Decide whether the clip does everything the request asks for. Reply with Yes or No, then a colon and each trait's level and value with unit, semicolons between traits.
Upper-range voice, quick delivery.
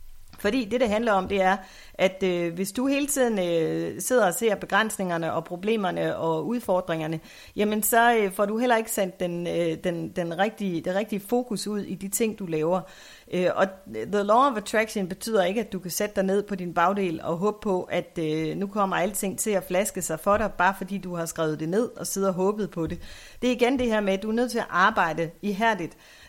Yes: high, 195 Hz; fast, 235 wpm